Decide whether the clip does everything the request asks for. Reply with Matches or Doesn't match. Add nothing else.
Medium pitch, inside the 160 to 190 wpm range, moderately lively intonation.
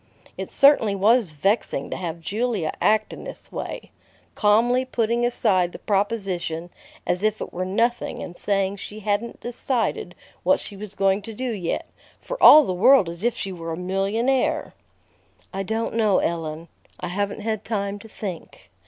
Doesn't match